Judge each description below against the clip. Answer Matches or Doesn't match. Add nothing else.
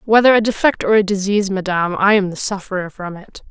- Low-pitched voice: Doesn't match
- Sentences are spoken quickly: Matches